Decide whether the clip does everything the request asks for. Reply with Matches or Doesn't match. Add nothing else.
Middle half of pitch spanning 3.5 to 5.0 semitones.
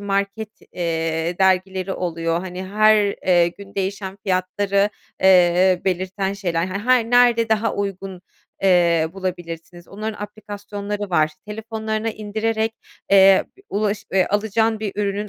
Doesn't match